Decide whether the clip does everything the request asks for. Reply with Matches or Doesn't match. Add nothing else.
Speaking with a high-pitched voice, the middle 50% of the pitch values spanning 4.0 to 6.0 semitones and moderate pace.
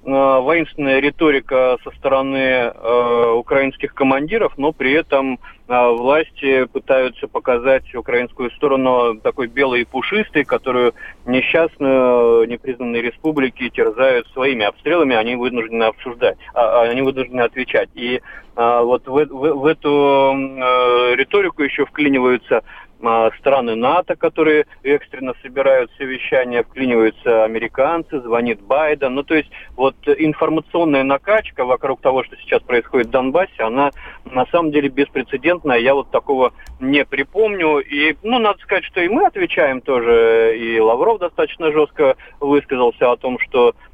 Doesn't match